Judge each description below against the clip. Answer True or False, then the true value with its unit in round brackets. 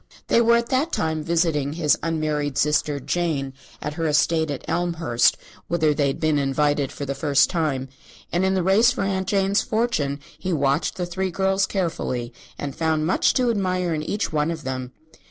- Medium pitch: True (160 Hz)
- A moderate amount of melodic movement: True (4.5 semitones)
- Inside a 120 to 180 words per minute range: False (190 wpm)